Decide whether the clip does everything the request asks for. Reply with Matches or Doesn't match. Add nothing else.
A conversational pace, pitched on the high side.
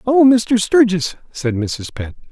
Matches